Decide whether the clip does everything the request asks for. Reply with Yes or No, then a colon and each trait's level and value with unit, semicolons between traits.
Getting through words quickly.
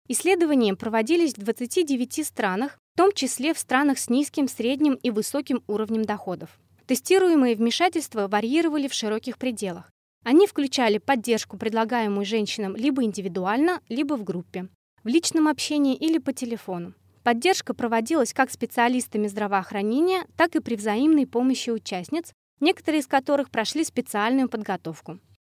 No: average, 130 wpm